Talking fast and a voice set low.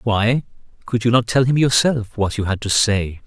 Yes: fast, 240 wpm; low, 115 Hz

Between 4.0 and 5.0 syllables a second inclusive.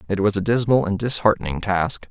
No: 5.7 syllables/s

